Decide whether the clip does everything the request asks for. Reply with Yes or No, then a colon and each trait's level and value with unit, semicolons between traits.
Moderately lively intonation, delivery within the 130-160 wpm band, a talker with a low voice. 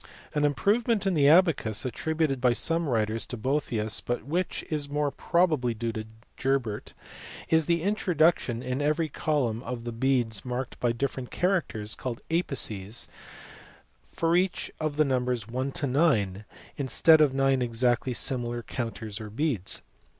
Yes: average, 5.0 semitones; average, 150 wpm; low, 130 Hz